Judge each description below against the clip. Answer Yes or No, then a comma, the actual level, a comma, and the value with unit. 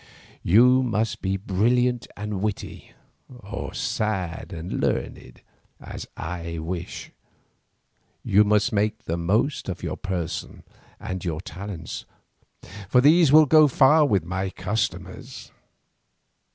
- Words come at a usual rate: No, slow, 110 wpm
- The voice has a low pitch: Yes, low, 100 Hz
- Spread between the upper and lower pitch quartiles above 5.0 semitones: Yes, wide, 5.4 semitones